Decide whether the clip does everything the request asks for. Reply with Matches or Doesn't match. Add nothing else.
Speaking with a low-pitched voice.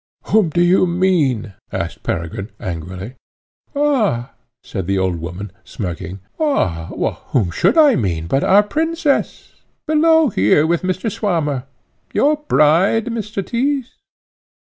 Doesn't match